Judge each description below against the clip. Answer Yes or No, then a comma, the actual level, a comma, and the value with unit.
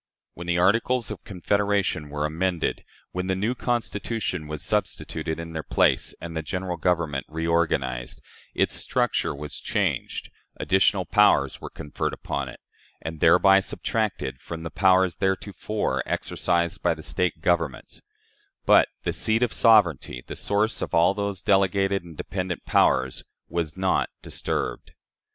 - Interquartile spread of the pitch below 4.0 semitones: Yes, average, 3.6 semitones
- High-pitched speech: No, very low, 90 Hz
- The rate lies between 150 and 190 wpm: No, average, 140 wpm